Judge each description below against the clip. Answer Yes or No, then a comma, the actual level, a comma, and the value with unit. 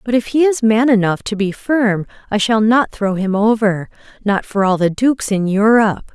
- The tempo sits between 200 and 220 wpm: Yes, fast, 205 wpm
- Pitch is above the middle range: Yes, high, 215 Hz